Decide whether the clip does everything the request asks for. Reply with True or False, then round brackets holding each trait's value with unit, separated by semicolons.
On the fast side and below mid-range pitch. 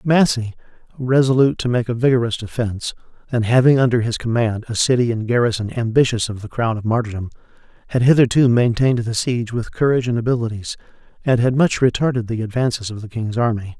False (180 wpm; 120 Hz)